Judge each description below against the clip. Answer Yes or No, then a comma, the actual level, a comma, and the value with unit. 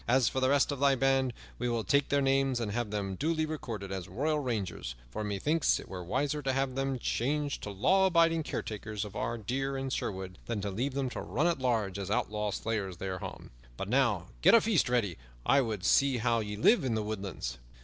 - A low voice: Yes, low, 120 Hz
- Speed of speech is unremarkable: No, fast, 220 wpm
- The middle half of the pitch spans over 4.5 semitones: Yes, average, 5.0 semitones